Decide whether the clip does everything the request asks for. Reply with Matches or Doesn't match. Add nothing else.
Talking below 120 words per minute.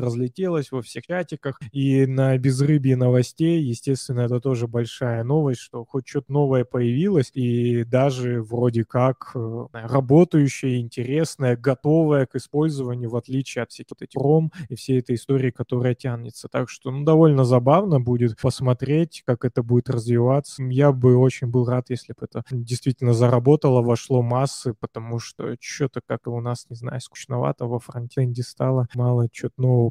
Doesn't match